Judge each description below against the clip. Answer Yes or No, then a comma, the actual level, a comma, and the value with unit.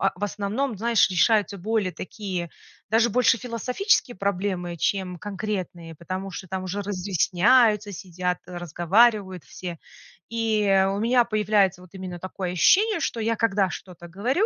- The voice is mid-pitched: No, high, 200 Hz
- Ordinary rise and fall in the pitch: Yes, average, 3.6 semitones